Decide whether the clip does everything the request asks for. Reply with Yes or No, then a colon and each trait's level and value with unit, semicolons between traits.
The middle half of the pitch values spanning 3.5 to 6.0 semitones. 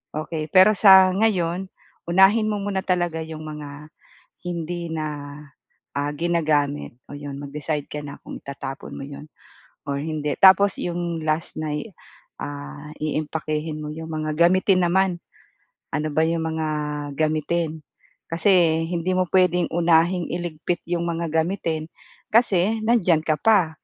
No: average, 2.8 semitones